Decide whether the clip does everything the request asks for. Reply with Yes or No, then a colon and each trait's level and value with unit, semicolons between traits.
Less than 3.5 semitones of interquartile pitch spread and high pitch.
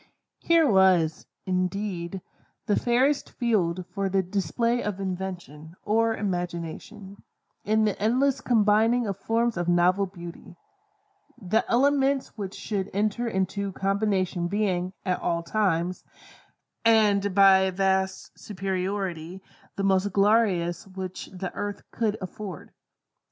Yes: average, 2.8 semitones; high, 195 Hz